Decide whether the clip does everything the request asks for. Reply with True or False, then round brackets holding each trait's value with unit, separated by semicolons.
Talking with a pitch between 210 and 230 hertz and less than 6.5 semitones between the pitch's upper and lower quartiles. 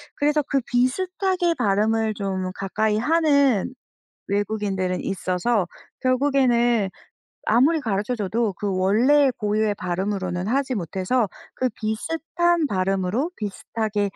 True (220 Hz; 5.3 semitones)